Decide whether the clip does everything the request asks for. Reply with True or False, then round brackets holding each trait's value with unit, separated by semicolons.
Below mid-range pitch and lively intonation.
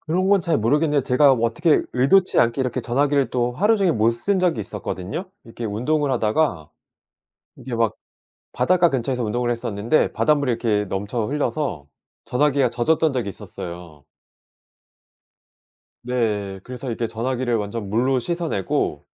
False (125 Hz; 5.0 semitones)